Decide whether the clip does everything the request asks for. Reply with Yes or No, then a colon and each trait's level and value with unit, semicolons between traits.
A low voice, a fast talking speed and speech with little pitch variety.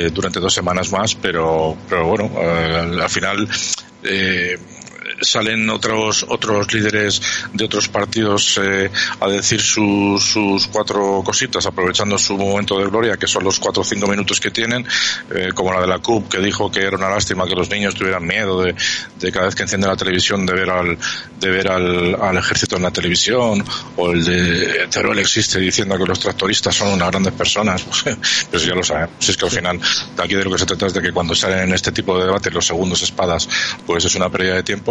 Yes: very low, 95 Hz; fast, 215 wpm; narrow, 2.0 semitones